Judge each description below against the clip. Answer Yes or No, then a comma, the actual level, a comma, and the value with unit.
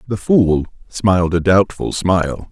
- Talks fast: No, average, 145 wpm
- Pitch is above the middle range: No, very low, 95 Hz